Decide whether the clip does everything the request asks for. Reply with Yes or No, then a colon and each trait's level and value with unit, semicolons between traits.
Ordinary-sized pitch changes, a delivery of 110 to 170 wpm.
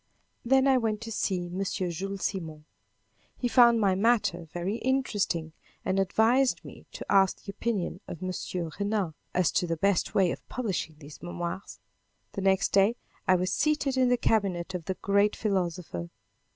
Yes: average, 4.2 semitones; average, 165 wpm